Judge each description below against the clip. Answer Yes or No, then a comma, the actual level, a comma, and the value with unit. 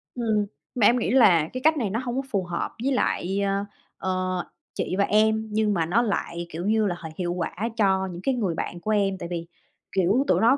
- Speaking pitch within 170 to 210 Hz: Yes, high, 200 Hz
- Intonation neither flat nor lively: Yes, average, 4.0 semitones